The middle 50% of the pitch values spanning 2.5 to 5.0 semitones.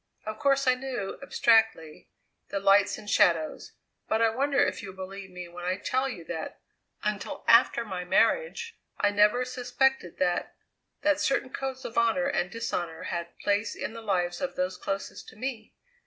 No: wide, 5.6 semitones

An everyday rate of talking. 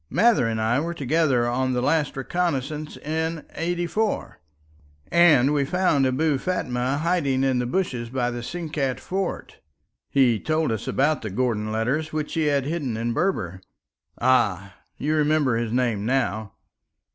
Yes: average, 150 wpm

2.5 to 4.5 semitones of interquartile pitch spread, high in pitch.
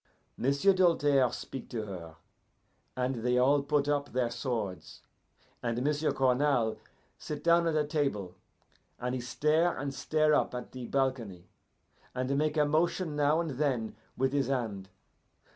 No: average, 3.5 semitones; low, 135 Hz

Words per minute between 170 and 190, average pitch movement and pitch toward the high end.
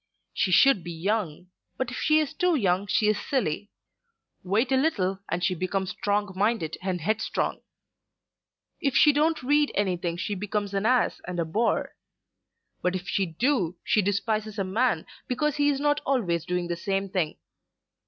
No: average, 175 wpm; wide, 5.9 semitones; high, 205 Hz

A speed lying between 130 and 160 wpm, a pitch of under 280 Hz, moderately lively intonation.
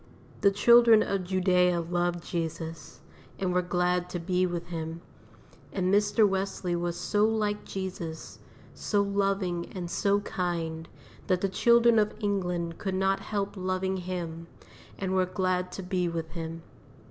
No: average, 145 wpm; medium, 185 Hz; narrow, 2.3 semitones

